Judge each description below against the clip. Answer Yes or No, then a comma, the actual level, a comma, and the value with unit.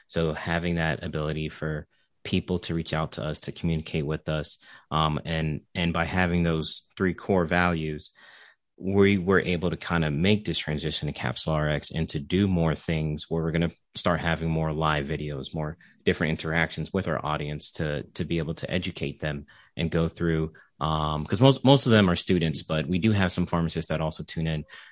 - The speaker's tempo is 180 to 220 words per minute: Yes, average, 200 wpm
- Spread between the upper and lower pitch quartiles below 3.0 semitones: Yes, narrow, 2.4 semitones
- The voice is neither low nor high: No, very low, 80 Hz